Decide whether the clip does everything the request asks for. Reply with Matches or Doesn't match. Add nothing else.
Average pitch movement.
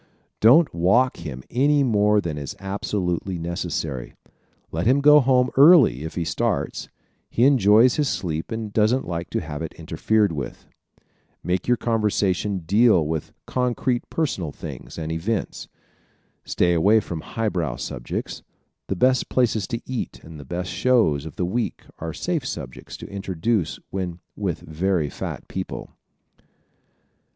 Doesn't match